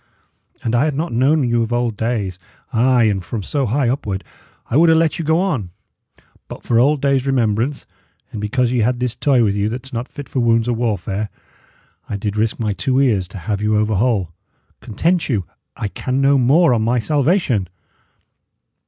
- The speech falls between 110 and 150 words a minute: No, average, 200 wpm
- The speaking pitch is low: Yes, low, 120 Hz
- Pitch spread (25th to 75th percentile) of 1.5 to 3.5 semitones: No, average, 4.2 semitones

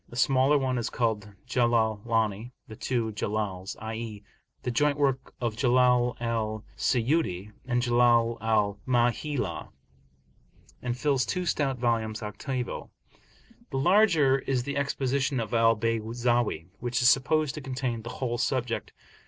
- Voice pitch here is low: Yes, low, 120 Hz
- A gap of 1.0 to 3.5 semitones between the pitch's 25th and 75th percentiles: Yes, average, 2.8 semitones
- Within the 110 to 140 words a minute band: Yes, slow, 135 wpm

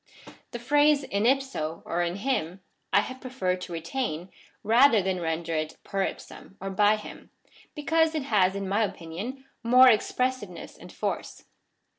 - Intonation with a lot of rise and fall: Yes, wide, 6.3 semitones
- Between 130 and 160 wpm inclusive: Yes, average, 145 wpm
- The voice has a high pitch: Yes, high, 210 Hz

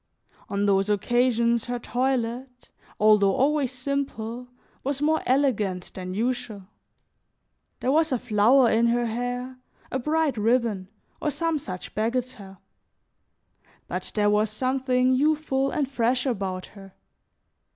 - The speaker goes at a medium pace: No, slow, 120 wpm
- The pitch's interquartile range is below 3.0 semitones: No, average, 3.7 semitones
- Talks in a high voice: Yes, high, 245 Hz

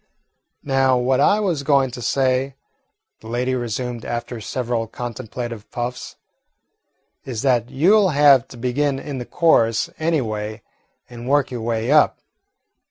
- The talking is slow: No, average, 145 wpm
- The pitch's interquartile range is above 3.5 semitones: No, average, 2.8 semitones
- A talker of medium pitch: No, low, 125 Hz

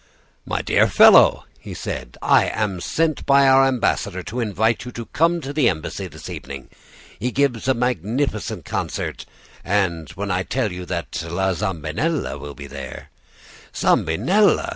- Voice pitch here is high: No, low, 105 Hz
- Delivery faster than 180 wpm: No, average, 160 wpm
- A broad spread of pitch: Yes, wide, 7.5 semitones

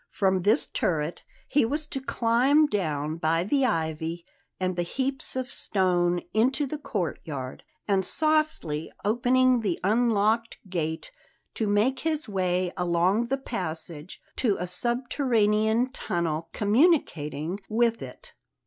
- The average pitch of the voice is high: Yes, high, 205 Hz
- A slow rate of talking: Yes, slow, 125 wpm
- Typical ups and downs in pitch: No, wide, 6.6 semitones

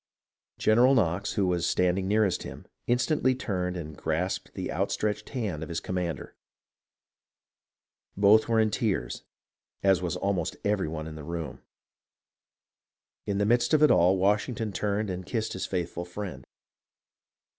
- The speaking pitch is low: Yes, very low, 95 Hz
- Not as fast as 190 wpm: Yes, average, 145 wpm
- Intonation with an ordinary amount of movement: Yes, average, 3.6 semitones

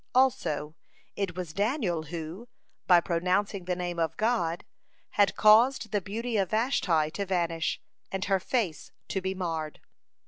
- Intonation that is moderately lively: Yes, average, 4.1 semitones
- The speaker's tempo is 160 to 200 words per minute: No, average, 150 wpm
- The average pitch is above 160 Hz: Yes, medium, 185 Hz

